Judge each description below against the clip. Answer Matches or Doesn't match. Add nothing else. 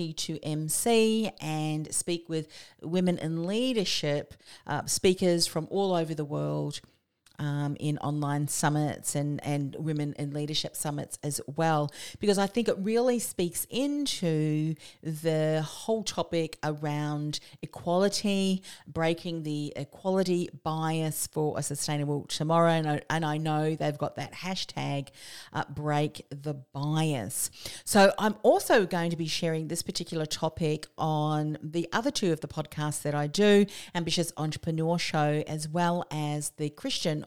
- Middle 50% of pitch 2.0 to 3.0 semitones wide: Matches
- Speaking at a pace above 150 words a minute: Doesn't match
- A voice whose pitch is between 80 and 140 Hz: Doesn't match